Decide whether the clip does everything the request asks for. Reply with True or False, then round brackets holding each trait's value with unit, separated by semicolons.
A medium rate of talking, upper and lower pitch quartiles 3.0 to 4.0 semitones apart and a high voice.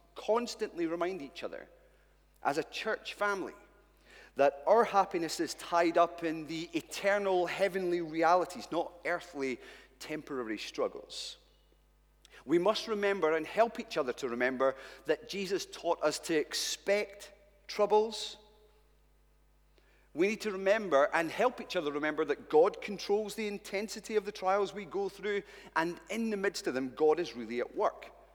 False (150 wpm; 4.8 semitones; 195 Hz)